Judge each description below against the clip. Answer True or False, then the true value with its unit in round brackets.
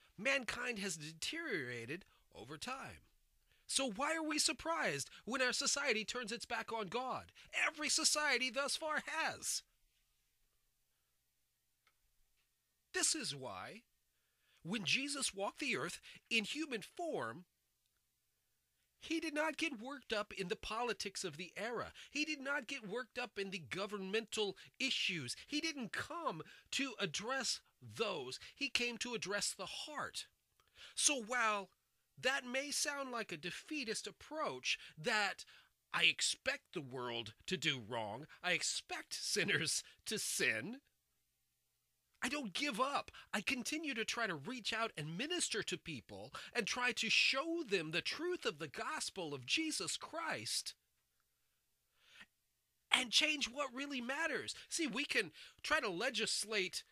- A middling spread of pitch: False (6.2 semitones)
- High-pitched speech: True (250 Hz)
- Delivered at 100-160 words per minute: True (135 wpm)